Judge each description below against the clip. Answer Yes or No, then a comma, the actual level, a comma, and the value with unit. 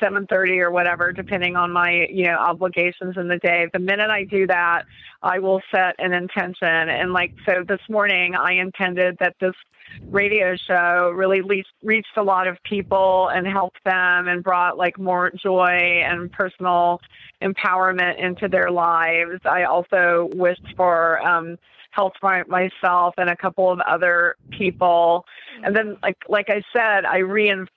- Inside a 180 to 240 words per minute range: No, average, 160 wpm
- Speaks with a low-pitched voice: No, medium, 185 Hz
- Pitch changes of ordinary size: No, narrow, 1.5 semitones